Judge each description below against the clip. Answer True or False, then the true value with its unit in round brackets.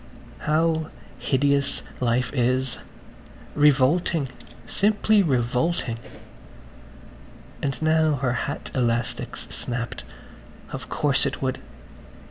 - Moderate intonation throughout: True (3.9 semitones)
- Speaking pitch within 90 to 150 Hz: True (140 Hz)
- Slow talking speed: True (80 wpm)